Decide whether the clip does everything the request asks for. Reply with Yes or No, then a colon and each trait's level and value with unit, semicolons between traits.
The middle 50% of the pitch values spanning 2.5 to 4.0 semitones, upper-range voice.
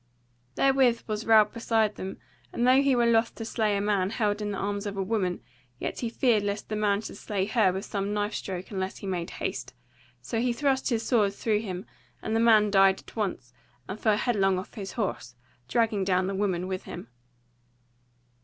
Yes: average, 2.8 semitones; high, 210 Hz